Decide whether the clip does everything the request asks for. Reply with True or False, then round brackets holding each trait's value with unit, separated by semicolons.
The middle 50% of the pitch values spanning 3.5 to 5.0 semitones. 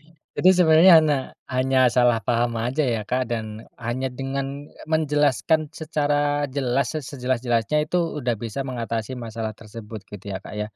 True (4.1 semitones)